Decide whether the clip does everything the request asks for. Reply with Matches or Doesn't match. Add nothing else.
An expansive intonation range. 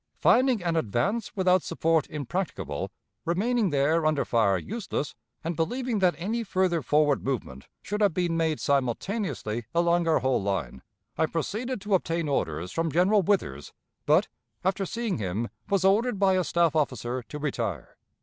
Matches